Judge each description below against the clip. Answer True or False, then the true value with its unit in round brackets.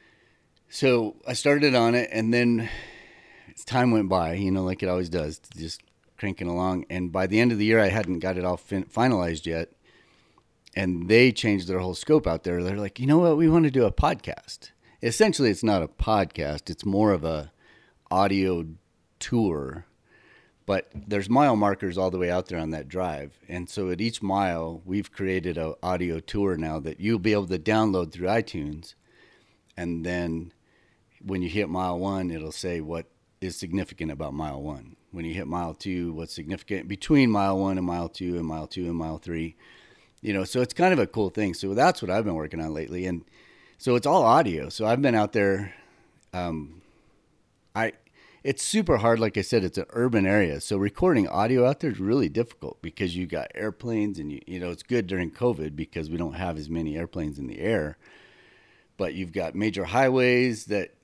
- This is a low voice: True (95 Hz)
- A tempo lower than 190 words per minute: False (200 wpm)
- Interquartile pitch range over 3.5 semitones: True (4.0 semitones)